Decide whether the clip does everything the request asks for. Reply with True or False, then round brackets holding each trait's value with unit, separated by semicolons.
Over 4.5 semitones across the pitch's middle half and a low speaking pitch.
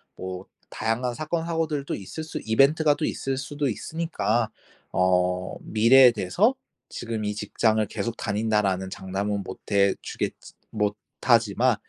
True (5.4 semitones; 110 Hz)